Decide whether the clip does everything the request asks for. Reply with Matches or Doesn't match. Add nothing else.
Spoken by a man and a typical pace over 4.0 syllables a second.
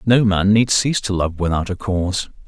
Matches